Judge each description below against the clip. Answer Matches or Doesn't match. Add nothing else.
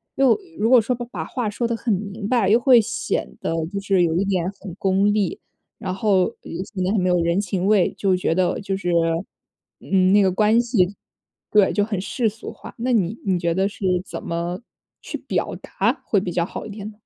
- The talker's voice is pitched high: Matches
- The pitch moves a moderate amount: Matches